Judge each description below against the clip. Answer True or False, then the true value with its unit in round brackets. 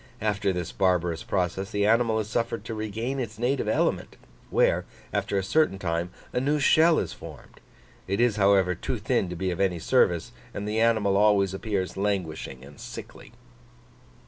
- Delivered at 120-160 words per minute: False (170 wpm)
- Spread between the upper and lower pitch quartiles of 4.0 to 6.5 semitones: False (3.4 semitones)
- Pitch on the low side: True (100 Hz)